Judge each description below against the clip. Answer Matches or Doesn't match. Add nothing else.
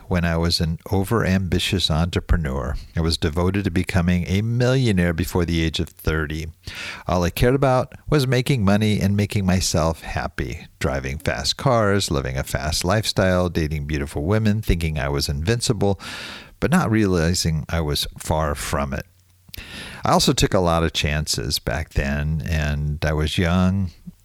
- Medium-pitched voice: Doesn't match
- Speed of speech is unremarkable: Matches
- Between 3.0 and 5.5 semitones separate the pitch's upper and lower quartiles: Matches